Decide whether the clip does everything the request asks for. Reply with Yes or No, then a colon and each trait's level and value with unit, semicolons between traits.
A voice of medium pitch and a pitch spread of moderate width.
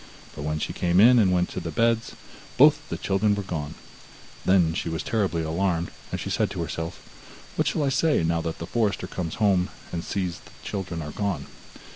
No: very low, 90 Hz; average, 3.8 semitones